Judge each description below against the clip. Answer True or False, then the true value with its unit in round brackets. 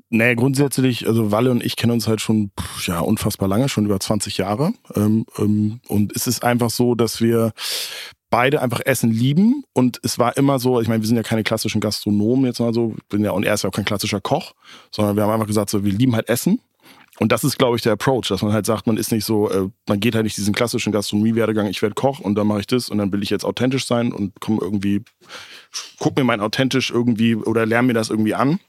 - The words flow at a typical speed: False (240 wpm)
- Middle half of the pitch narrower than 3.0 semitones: True (2.6 semitones)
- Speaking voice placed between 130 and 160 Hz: False (110 Hz)